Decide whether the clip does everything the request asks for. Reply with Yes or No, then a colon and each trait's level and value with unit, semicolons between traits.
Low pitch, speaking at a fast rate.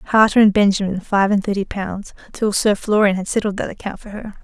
No: high, 200 Hz; fast, 215 wpm